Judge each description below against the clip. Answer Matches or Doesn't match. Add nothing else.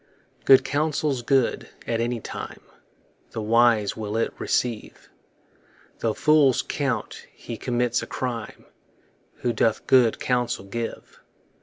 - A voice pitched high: Doesn't match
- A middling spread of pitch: Doesn't match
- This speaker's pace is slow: Matches